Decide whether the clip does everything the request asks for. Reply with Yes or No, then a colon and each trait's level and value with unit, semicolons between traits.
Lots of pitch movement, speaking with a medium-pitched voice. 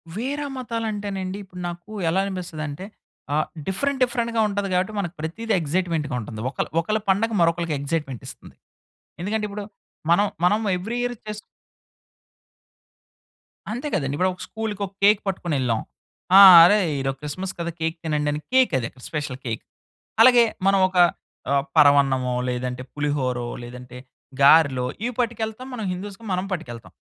Yes: wide, 6.8 semitones; medium, 180 Hz